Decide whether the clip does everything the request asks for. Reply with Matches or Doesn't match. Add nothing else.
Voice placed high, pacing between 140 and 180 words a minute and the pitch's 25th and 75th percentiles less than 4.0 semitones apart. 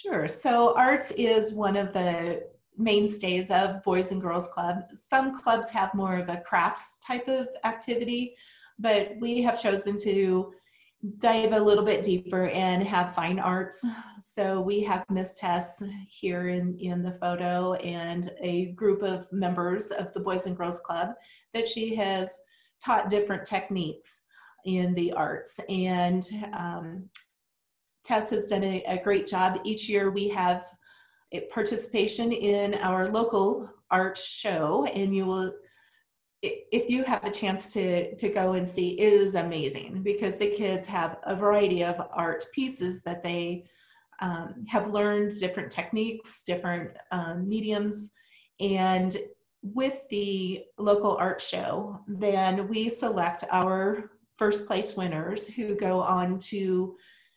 Matches